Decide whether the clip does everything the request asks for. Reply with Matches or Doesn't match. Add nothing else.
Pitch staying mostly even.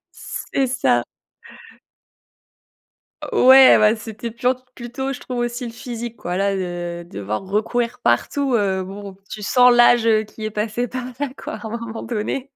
Doesn't match